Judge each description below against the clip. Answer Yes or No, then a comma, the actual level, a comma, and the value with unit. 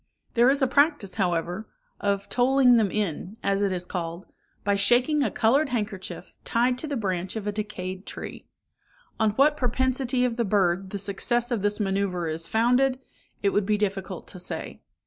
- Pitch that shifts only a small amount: No, average, 4.5 semitones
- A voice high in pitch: Yes, high, 210 Hz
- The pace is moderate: Yes, average, 180 wpm